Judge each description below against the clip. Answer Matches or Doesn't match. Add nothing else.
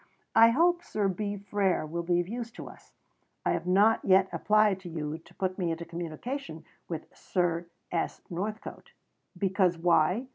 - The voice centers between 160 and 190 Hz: Matches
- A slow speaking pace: Doesn't match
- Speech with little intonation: Doesn't match